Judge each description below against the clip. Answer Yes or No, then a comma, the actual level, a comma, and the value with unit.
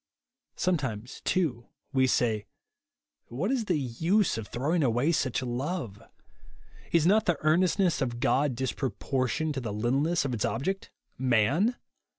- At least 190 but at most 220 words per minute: No, average, 145 wpm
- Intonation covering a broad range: Yes, wide, 6.0 semitones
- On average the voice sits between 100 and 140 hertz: Yes, low, 135 Hz